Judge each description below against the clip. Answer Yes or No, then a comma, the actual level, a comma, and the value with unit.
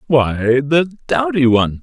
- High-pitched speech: No, low, 135 Hz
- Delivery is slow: Yes, slow, 130 wpm